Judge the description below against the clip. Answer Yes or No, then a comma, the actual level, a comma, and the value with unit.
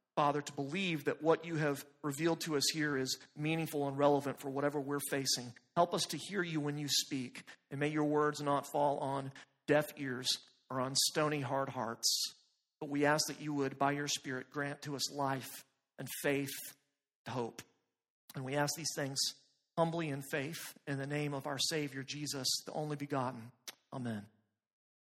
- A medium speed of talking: Yes, average, 185 wpm